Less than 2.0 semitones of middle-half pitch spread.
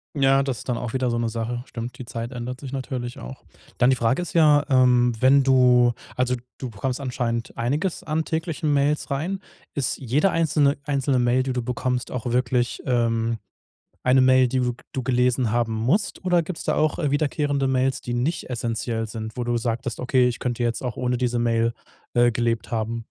No: narrow, 2.5 semitones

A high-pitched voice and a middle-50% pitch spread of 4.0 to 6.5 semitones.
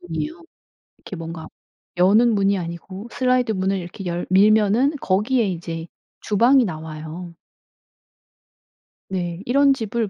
Yes: high, 195 Hz; average, 5.2 semitones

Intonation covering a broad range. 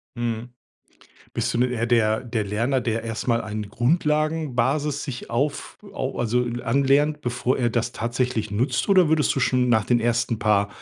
No: average, 2.8 semitones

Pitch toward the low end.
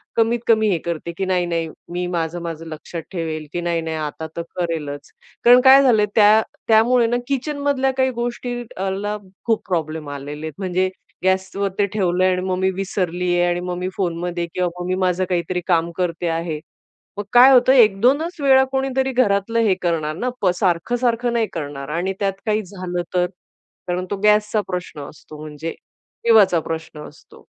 No: medium, 185 Hz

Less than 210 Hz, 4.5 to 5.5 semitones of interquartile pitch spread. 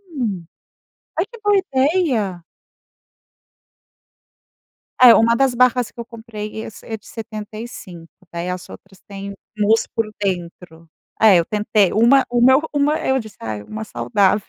No: high, 215 Hz; average, 5.0 semitones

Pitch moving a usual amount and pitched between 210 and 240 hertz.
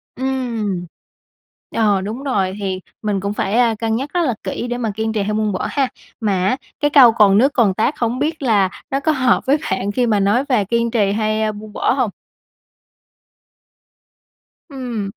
Yes: average, 3.9 semitones; high, 220 Hz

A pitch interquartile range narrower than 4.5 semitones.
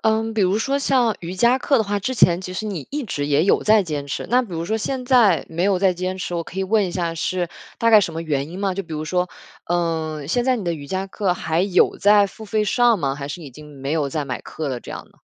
No: average, 5.1 semitones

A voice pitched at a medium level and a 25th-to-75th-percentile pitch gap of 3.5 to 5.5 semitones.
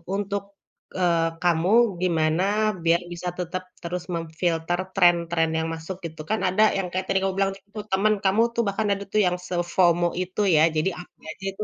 No: medium, 180 Hz; narrow, 2.4 semitones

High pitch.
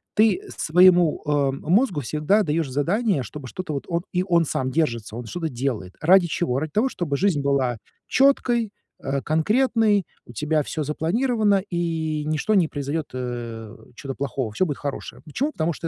No: medium, 155 Hz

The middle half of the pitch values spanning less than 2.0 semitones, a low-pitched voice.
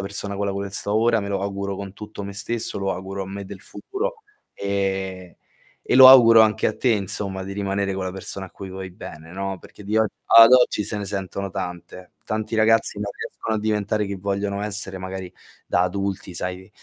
Yes: narrow, 1.6 semitones; low, 100 Hz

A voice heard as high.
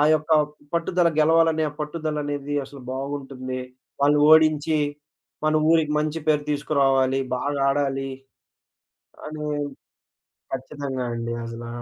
No: medium, 145 Hz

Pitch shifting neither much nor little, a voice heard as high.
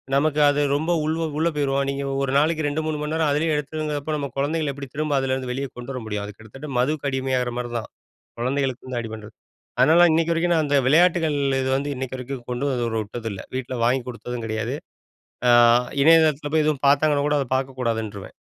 No: average, 3.6 semitones; medium, 140 Hz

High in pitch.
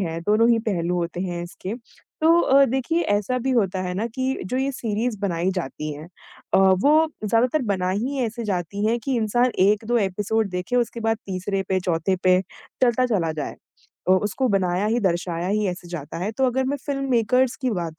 Yes: high, 210 Hz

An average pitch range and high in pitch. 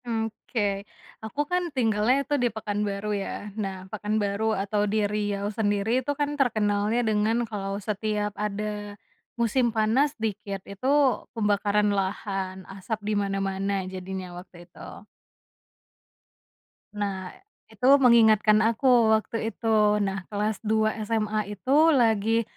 No: narrow, 1.9 semitones; high, 210 Hz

